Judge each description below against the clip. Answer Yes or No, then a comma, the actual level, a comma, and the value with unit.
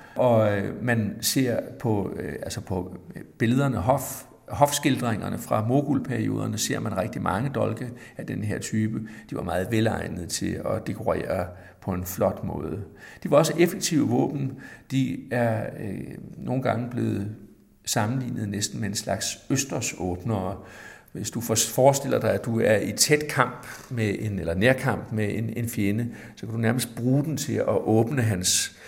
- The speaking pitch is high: No, low, 115 Hz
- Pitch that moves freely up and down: No, average, 3.7 semitones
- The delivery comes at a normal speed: Yes, average, 160 wpm